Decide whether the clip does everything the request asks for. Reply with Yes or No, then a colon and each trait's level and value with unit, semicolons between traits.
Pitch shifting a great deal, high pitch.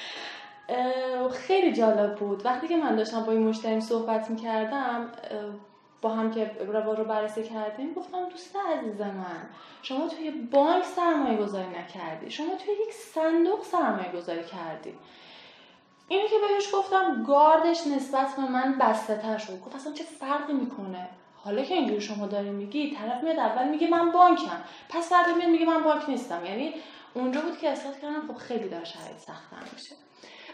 Yes: wide, 7.1 semitones; very high, 260 Hz